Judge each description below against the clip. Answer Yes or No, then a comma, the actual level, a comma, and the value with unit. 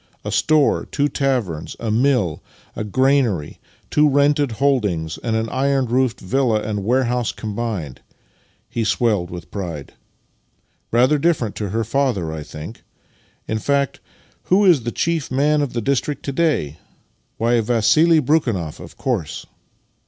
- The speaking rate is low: No, average, 145 wpm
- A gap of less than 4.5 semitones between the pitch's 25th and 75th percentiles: No, average, 5.1 semitones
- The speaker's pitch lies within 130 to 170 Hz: No, low, 120 Hz